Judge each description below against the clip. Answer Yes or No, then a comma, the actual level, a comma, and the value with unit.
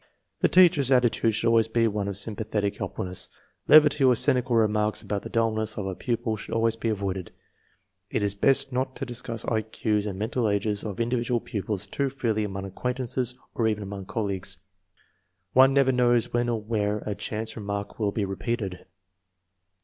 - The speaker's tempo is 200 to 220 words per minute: No, average, 180 wpm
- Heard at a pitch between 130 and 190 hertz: No, low, 110 Hz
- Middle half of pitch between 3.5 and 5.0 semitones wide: No, average, 2.9 semitones